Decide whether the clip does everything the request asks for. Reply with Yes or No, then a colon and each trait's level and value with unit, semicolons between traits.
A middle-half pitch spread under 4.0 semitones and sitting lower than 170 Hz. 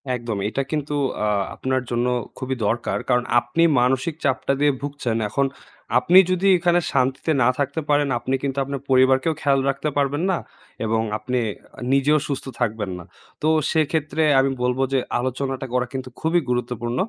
Yes: average, 2.7 semitones; low, 135 Hz